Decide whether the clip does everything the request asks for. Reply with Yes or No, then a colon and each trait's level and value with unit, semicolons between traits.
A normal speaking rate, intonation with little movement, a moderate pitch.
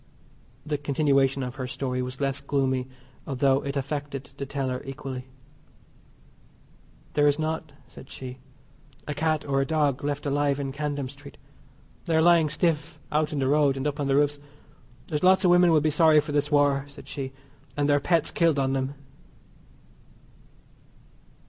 Yes: average, 170 wpm; narrow, 1.8 semitones; medium, 145 Hz